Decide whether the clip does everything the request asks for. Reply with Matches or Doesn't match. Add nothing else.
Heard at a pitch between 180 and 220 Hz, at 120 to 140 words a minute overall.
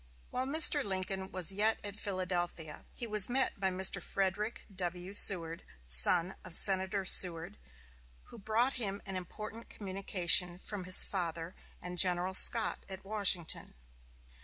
Matches